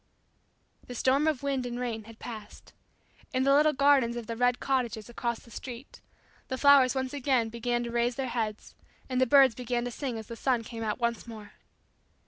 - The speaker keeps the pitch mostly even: Yes, narrow, 2.2 semitones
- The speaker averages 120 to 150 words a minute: No, average, 200 wpm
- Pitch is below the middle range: No, high, 245 Hz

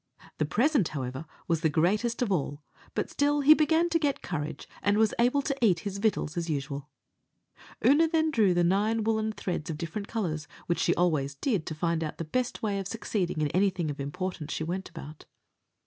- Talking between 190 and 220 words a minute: Yes, average, 200 wpm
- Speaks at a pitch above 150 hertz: Yes, medium, 185 Hz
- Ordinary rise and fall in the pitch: No, wide, 6.3 semitones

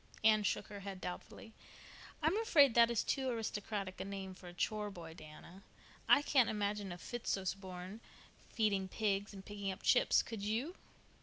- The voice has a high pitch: Yes, high, 205 Hz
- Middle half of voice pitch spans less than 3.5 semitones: Yes, average, 2.8 semitones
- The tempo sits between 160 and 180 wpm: Yes, average, 165 wpm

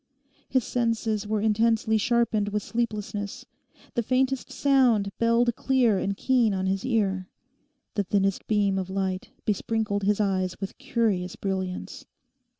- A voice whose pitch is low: No, high, 210 Hz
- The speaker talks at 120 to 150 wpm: Yes, slow, 135 wpm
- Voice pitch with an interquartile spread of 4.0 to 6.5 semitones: No, average, 3.0 semitones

